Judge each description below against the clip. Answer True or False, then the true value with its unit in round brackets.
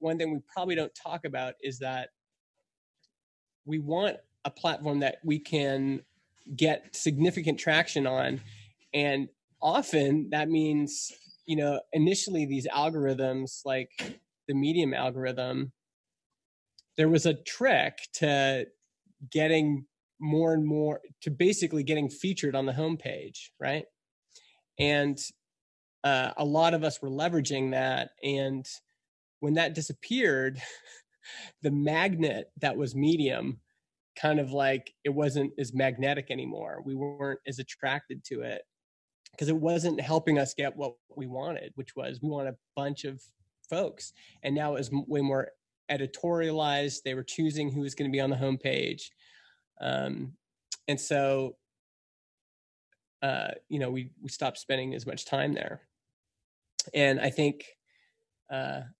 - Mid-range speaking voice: True (145 Hz)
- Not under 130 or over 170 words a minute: True (135 wpm)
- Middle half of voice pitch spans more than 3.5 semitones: False (2.7 semitones)